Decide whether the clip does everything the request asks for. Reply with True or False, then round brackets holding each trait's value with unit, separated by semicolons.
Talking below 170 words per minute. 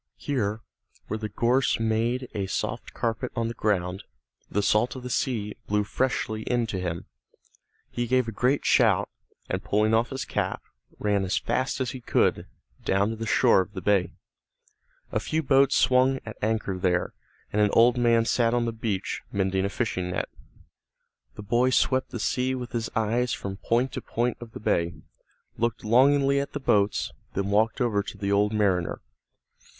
False (180 wpm)